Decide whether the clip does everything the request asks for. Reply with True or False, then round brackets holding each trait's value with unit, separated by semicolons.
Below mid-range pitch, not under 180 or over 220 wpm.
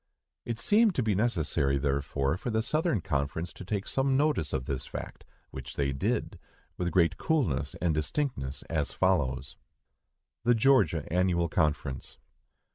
False (85 Hz; 145 wpm)